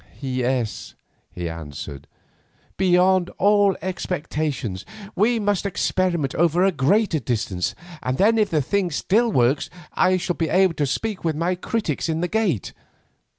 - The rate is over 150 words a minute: No, average, 145 wpm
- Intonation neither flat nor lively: No, wide, 6.5 semitones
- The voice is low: No, medium, 175 Hz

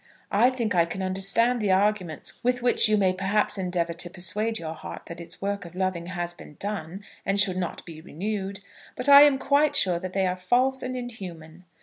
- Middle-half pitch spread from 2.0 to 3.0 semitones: No, average, 3.8 semitones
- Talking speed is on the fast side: Yes, fast, 210 wpm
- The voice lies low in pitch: No, high, 190 Hz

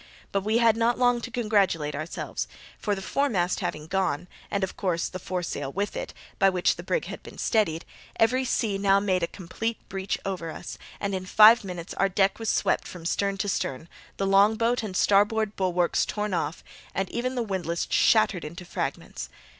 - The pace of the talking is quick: No, average, 190 wpm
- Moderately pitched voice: No, high, 195 Hz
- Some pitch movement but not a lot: Yes, average, 3.4 semitones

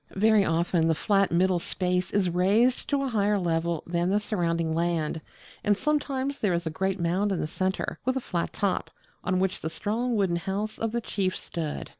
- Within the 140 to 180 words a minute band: No, average, 200 wpm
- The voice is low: No, high, 190 Hz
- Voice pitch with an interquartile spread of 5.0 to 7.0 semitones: No, average, 3.6 semitones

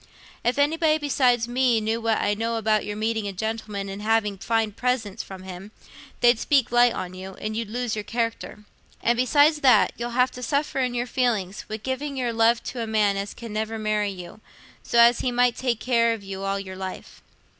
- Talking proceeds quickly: Yes, fast, 210 wpm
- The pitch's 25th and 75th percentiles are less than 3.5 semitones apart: Yes, average, 2.9 semitones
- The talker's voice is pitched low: No, high, 225 Hz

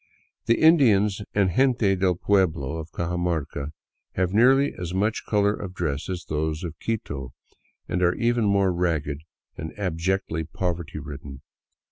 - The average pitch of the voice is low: Yes, very low, 90 Hz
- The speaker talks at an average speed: Yes, average, 145 wpm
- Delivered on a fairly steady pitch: No, average, 4.3 semitones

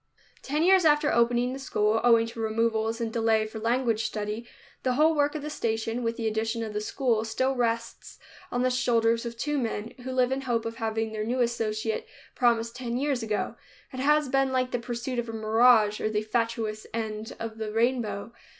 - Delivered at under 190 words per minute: No, fast, 205 wpm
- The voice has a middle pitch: No, high, 230 Hz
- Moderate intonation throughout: No, narrow, 2.3 semitones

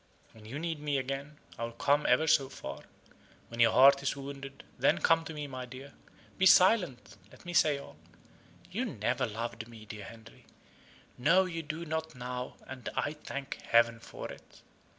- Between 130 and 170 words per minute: No, average, 180 wpm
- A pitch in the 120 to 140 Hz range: Yes, low, 135 Hz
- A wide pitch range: No, average, 4.6 semitones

